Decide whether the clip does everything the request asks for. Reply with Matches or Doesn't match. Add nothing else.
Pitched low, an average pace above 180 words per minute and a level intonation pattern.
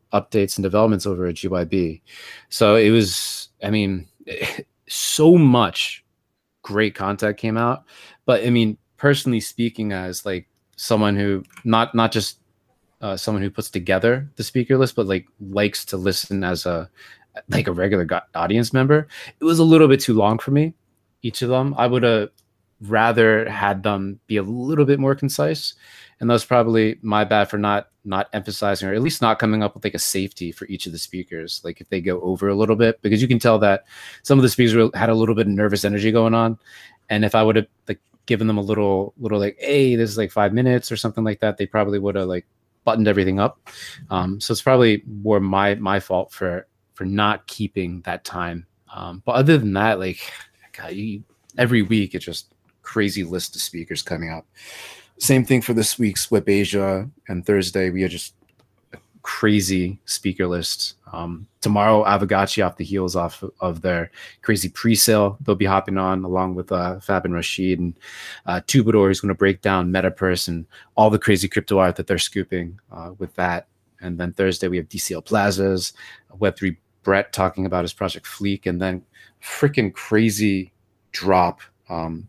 Doesn't match